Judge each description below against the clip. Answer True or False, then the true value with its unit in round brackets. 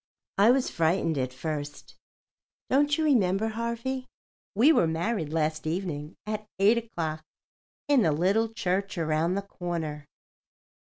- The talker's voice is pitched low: False (185 Hz)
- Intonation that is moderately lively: False (6.2 semitones)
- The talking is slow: True (130 wpm)